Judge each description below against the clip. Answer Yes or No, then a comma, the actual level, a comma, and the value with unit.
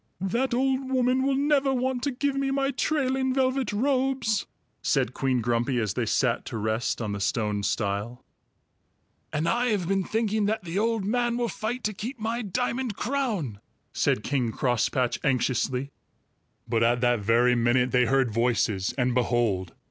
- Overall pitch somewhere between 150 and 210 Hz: Yes, medium, 185 Hz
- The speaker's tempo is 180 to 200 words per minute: No, average, 165 wpm